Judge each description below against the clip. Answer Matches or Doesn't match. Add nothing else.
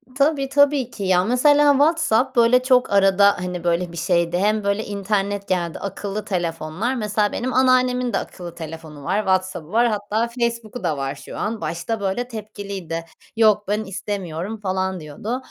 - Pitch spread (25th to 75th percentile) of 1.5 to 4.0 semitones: Doesn't match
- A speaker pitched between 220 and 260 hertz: Doesn't match